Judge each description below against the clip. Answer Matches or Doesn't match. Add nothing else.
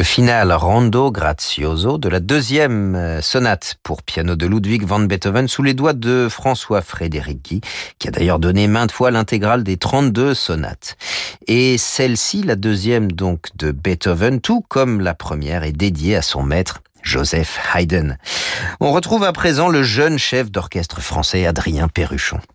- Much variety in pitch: Matches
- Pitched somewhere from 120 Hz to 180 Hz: Doesn't match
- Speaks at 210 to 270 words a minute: Doesn't match